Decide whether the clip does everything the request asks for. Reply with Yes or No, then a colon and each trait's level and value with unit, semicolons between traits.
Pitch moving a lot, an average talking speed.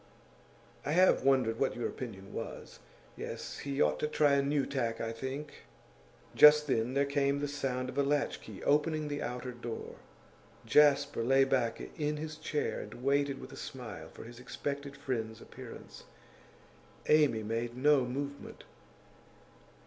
No: average, 3.1 semitones; average, 155 wpm